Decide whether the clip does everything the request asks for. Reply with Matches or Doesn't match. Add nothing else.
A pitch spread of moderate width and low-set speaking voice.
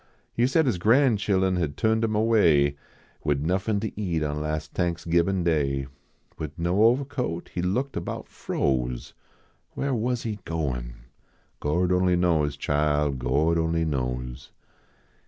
Doesn't match